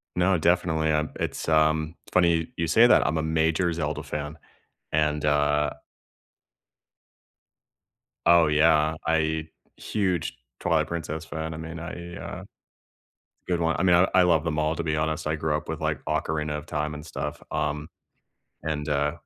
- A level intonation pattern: Yes, narrow, 1.7 semitones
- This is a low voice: Yes, very low, 80 Hz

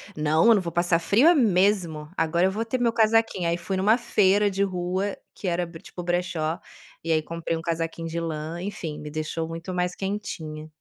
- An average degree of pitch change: Yes, average, 3.4 semitones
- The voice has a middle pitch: Yes, medium, 175 Hz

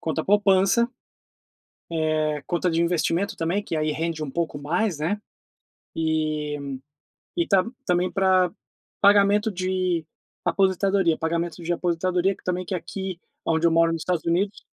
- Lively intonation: No, average, 2.8 semitones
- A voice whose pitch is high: No, medium, 175 Hz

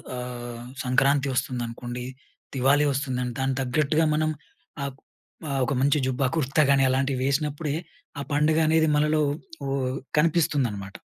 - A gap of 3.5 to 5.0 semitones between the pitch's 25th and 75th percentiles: No, average, 2.9 semitones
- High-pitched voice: No, low, 135 Hz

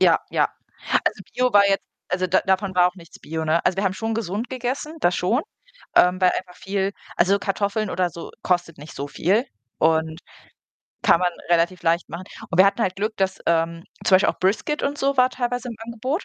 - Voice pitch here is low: No, high, 190 Hz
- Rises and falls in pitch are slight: No, average, 4.2 semitones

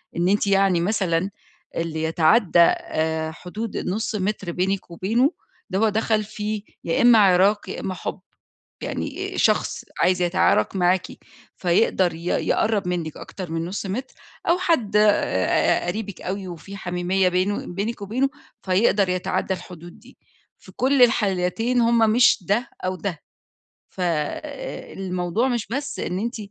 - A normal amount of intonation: Yes, average, 3.5 semitones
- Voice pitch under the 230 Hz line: Yes, high, 190 Hz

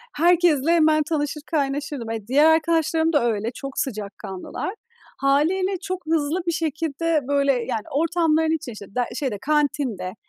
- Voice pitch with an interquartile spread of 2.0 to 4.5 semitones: Yes, average, 3.7 semitones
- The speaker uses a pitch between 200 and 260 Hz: No, very high, 295 Hz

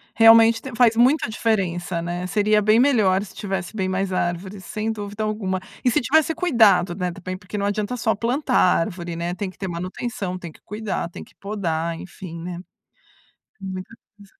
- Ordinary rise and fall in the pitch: Yes, average, 3.5 semitones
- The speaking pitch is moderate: No, high, 200 Hz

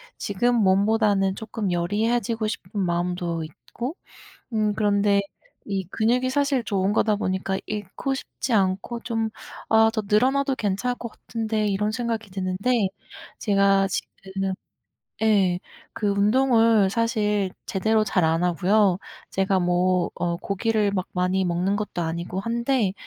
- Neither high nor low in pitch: No, high, 205 Hz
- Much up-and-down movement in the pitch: No, average, 3.0 semitones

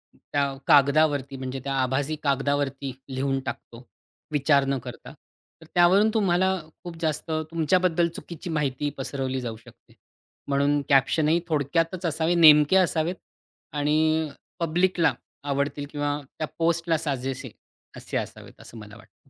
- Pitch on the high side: No, medium, 150 Hz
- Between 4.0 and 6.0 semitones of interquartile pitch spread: No, average, 3.3 semitones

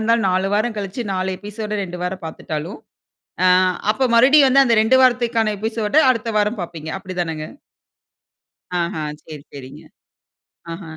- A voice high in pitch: Yes, high, 205 Hz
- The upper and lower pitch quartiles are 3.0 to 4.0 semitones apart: No, average, 4.5 semitones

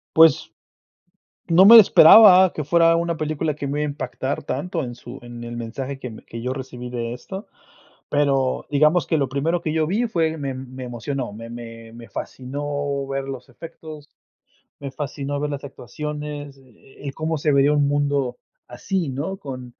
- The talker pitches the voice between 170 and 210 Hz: No, medium, 140 Hz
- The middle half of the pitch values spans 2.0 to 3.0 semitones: No, average, 3.4 semitones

